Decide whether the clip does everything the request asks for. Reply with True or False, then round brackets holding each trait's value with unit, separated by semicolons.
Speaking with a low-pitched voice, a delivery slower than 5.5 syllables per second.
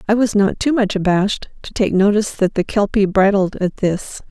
False (200 Hz; 5.3 syllables/s)